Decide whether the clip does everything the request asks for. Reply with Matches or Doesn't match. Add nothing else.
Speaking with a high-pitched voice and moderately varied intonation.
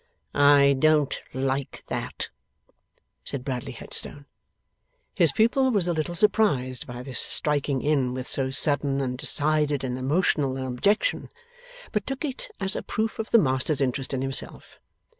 Doesn't match